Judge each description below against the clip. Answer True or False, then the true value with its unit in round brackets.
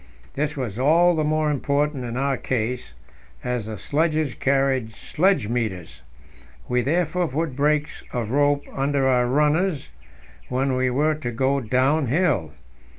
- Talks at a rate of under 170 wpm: True (140 wpm)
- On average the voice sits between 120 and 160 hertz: True (135 Hz)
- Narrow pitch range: False (3.5 semitones)